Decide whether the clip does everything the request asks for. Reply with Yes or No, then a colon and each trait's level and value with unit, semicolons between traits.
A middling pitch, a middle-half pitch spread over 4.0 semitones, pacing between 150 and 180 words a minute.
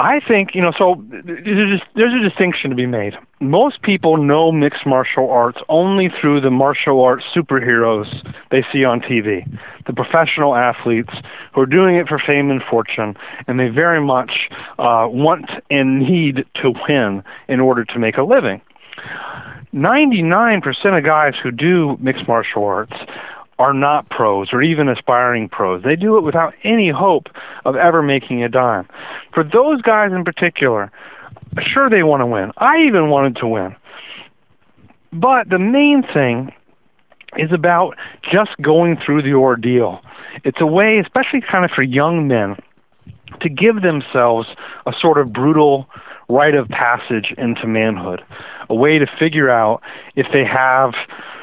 Yes: medium, 145 Hz; wide, 5.6 semitones; average, 160 wpm